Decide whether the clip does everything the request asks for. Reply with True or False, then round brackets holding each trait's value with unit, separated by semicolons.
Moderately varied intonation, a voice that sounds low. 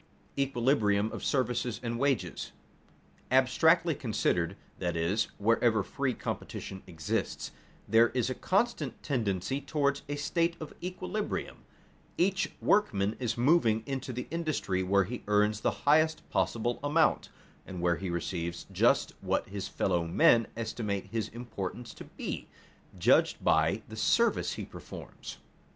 False (5.9 semitones; 120 Hz)